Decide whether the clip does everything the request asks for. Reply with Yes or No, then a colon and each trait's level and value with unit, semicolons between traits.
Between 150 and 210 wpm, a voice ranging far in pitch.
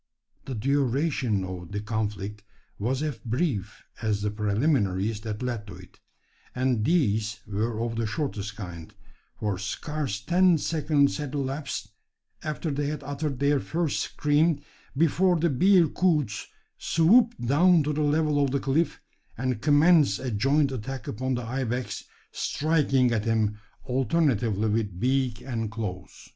No: average, 140 wpm; wide, 5.8 semitones